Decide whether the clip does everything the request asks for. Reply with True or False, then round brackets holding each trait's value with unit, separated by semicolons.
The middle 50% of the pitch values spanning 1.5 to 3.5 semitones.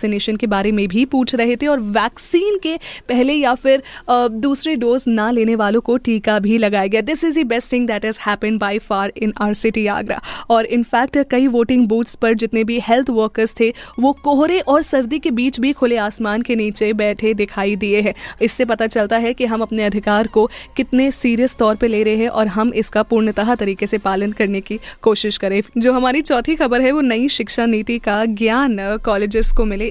True (2.8 semitones)